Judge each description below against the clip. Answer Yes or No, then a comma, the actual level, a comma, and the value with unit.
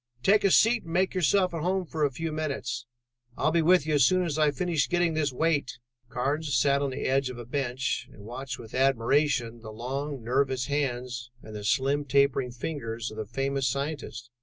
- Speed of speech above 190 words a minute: Yes, fast, 205 wpm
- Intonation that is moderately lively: Yes, average, 4.2 semitones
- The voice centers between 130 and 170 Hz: Yes, medium, 140 Hz